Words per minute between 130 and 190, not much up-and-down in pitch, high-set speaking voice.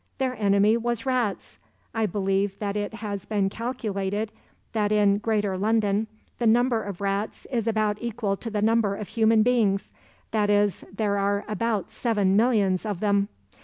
Yes: average, 165 wpm; narrow, 2.0 semitones; high, 210 Hz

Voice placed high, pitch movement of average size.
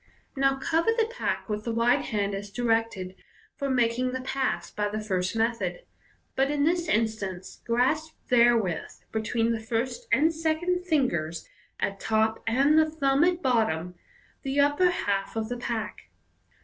Yes: high, 240 Hz; average, 5.0 semitones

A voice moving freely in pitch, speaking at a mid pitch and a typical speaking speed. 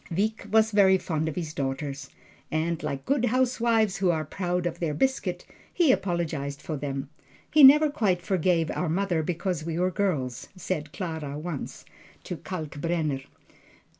No: average, 4.4 semitones; medium, 175 Hz; average, 155 wpm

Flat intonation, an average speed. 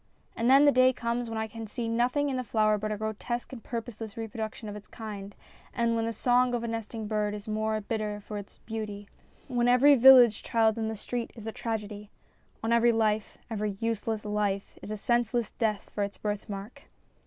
No: narrow, 2.1 semitones; fast, 210 wpm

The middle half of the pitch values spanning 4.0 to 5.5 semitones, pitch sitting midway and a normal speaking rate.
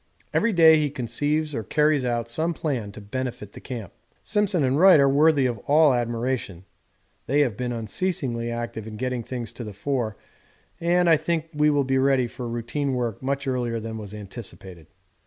No: average, 4.3 semitones; low, 130 Hz; average, 180 wpm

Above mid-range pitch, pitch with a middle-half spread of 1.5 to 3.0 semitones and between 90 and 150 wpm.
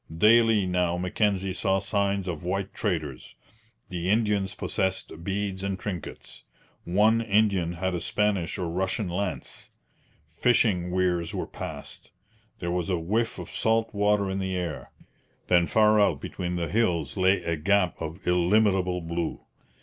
No: very low, 95 Hz; average, 2.7 semitones; average, 145 wpm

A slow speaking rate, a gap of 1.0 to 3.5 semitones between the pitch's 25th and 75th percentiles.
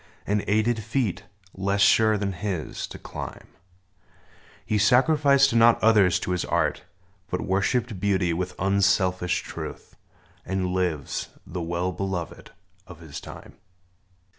Yes: slow, 125 wpm; average, 3.2 semitones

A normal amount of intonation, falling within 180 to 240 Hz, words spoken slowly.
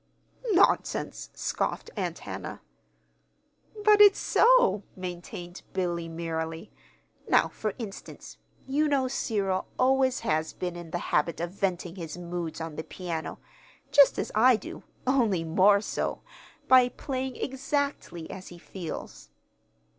No: wide, 7.2 semitones; high, 190 Hz; slow, 125 wpm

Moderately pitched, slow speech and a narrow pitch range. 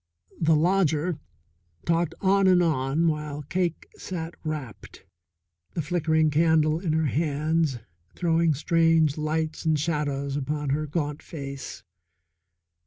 Yes: medium, 155 Hz; slow, 115 wpm; narrow, 2.1 semitones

